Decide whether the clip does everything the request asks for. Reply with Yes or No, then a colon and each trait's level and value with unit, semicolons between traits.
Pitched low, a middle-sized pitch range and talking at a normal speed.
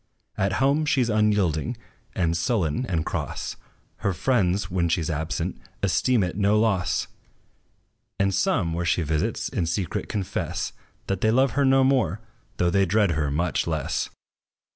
Yes: very low, 95 Hz; average, 4.6 semitones; average, 160 wpm